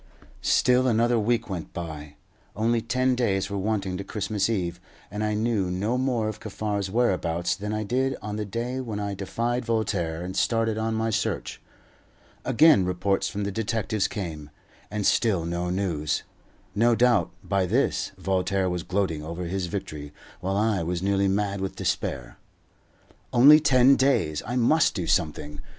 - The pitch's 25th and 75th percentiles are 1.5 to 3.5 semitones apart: No, average, 3.9 semitones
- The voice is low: Yes, low, 100 Hz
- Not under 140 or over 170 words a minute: Yes, average, 165 wpm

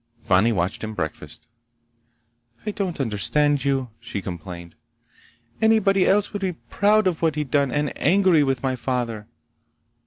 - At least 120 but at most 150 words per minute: Yes, average, 145 wpm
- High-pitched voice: No, medium, 140 Hz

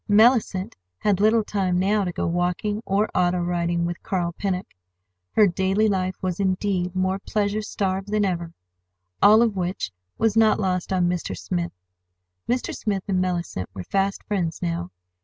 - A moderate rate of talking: Yes, average, 160 wpm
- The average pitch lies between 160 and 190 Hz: Yes, medium, 185 Hz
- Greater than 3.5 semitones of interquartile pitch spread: No, average, 2.7 semitones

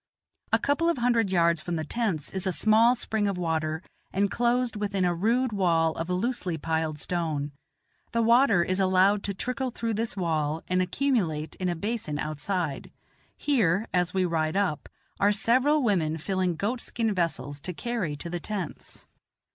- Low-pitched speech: No, medium, 185 Hz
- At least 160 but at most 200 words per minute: Yes, average, 170 wpm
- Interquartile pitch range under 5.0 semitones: No, wide, 5.6 semitones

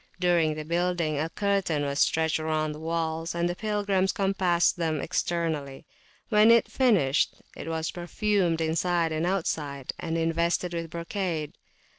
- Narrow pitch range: Yes, narrow, 2.3 semitones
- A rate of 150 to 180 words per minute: No, slow, 135 wpm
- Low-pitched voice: No, medium, 170 Hz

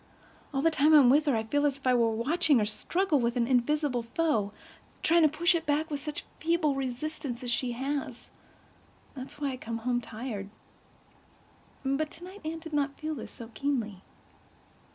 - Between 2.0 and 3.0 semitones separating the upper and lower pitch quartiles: No, average, 4.3 semitones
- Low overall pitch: No, very high, 275 Hz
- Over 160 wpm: Yes, average, 185 wpm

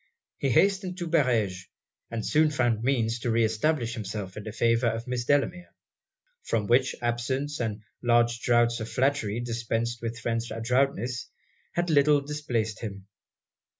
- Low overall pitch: Yes, low, 120 Hz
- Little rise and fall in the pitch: No, average, 3.4 semitones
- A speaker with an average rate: Yes, average, 150 wpm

